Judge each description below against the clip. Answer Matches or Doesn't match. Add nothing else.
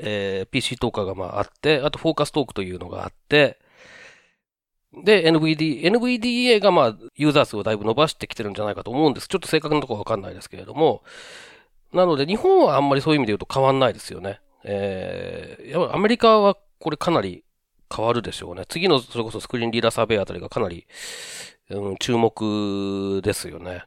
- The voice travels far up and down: Matches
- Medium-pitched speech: Doesn't match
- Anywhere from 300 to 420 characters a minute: Doesn't match